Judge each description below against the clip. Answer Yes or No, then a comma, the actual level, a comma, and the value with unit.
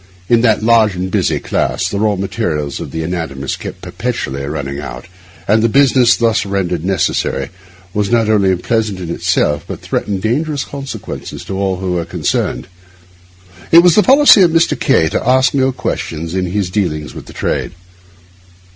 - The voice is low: Yes, low, 100 Hz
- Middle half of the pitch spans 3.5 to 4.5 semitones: No, wide, 5.6 semitones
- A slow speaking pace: No, average, 175 wpm